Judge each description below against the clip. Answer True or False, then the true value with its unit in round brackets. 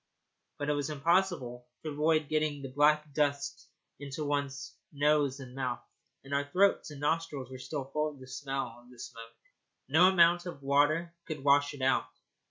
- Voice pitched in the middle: True (145 Hz)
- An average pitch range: False (2.2 semitones)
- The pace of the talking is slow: False (175 wpm)